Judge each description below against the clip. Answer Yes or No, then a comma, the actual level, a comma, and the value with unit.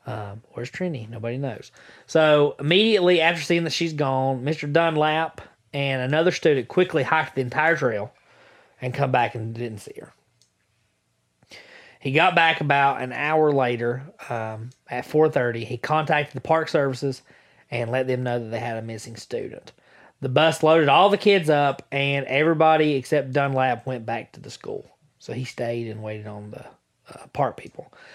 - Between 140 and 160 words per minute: No, average, 170 wpm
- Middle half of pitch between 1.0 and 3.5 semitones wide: No, average, 4.6 semitones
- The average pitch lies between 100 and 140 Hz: Yes, low, 135 Hz